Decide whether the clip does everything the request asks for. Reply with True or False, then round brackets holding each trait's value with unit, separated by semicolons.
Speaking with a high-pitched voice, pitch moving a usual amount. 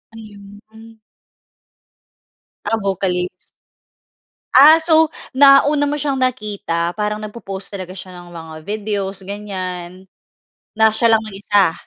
True (205 Hz; 3.2 semitones)